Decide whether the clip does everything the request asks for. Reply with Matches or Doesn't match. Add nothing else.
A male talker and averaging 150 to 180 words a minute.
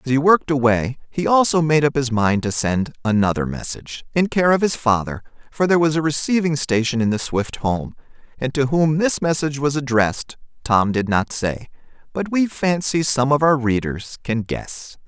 Doesn't match